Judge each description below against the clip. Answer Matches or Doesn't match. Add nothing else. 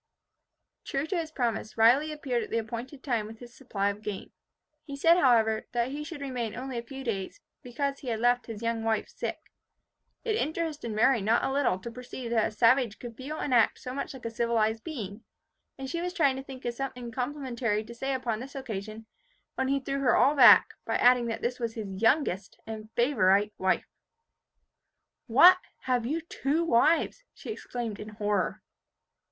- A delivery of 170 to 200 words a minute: Matches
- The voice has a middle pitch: Doesn't match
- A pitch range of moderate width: Matches